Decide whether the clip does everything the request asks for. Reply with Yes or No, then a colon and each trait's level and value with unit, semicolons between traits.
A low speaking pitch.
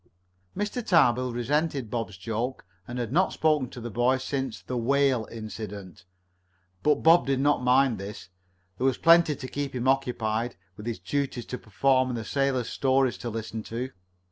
Yes: low, 125 Hz